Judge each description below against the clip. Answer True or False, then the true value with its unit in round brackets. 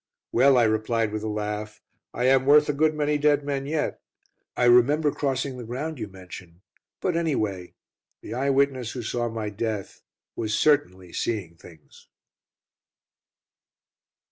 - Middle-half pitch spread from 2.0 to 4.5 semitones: False (5.0 semitones)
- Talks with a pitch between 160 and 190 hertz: False (120 Hz)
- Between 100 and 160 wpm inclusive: True (145 wpm)